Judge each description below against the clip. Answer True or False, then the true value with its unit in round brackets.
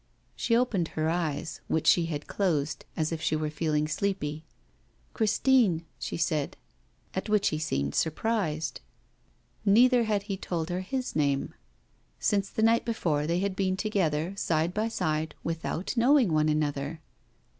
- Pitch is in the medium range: True (170 Hz)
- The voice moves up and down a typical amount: True (4.9 semitones)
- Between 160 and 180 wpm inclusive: False (150 wpm)